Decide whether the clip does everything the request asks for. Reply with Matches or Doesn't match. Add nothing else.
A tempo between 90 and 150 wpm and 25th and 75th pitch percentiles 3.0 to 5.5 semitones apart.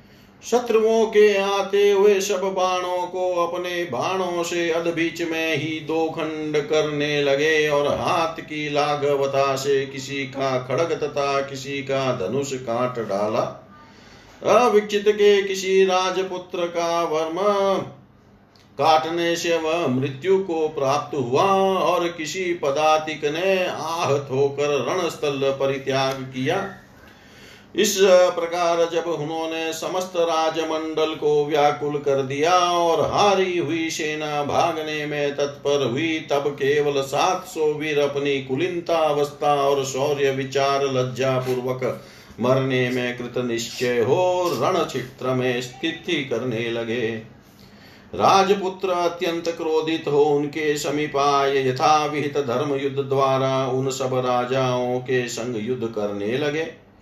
Matches